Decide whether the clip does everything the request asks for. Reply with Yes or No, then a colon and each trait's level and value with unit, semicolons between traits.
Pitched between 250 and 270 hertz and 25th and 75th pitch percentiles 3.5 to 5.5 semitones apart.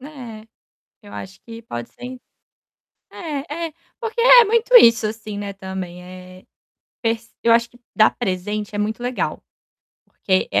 No: high, 225 Hz; average, 4.9 semitones